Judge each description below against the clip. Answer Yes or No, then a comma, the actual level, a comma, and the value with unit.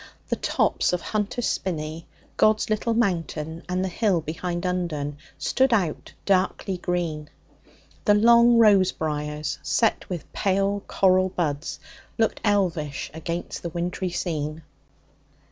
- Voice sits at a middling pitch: Yes, medium, 180 Hz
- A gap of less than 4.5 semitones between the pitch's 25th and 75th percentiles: Yes, average, 4.0 semitones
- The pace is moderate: No, slow, 125 wpm